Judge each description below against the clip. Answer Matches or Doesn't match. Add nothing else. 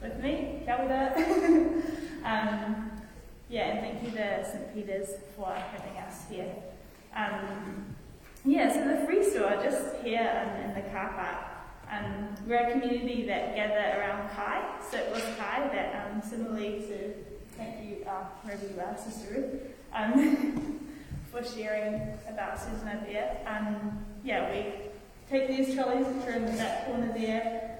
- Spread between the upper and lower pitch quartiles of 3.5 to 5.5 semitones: Matches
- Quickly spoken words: Doesn't match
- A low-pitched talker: Doesn't match